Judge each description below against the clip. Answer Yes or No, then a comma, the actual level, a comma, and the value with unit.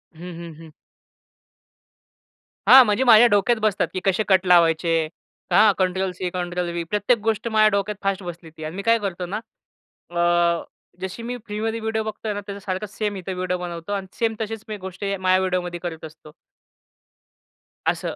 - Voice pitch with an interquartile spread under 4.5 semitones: Yes, average, 3.3 semitones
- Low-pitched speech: No, high, 190 Hz